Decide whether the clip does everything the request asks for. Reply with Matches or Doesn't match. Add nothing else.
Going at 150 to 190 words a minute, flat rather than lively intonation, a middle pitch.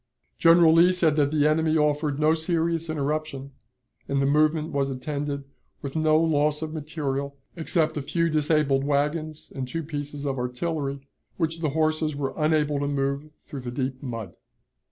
Matches